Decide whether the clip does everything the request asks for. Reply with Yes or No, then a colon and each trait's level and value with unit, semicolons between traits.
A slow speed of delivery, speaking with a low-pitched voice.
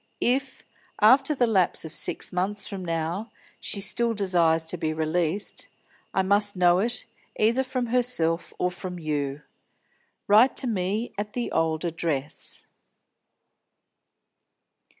No: slow, 130 wpm; medium, 185 Hz